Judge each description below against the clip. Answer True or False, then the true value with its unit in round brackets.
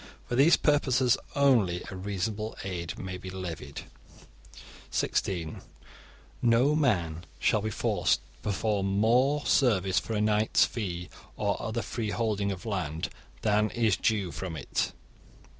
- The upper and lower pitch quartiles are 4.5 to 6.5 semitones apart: False (4.0 semitones)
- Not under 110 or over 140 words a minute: True (135 wpm)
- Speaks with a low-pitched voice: True (105 Hz)